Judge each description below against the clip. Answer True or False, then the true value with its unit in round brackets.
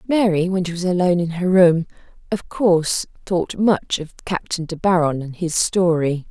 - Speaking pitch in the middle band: True (175 Hz)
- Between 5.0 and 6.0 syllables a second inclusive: False (4.8 syllables/s)